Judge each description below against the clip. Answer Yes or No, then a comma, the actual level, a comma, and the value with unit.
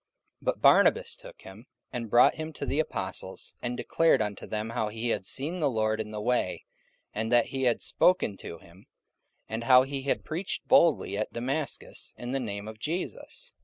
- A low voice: Yes, low, 120 Hz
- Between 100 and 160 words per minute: No, average, 195 wpm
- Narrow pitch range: No, average, 4.4 semitones